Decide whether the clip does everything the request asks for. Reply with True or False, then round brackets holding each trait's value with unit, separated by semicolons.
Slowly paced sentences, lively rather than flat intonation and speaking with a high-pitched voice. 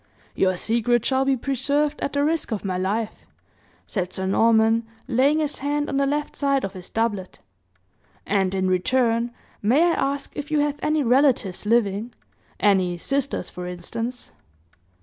False (160 wpm; 6.1 semitones; 235 Hz)